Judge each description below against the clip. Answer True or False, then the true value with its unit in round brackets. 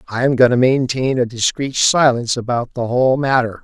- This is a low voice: True (125 Hz)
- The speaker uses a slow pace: False (200 wpm)